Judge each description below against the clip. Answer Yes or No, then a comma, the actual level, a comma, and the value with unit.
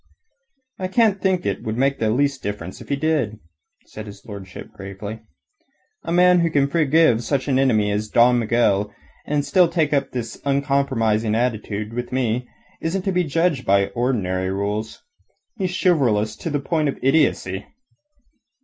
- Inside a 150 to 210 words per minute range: Yes, average, 160 wpm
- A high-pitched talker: No, low, 125 Hz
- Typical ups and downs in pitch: No, wide, 6.3 semitones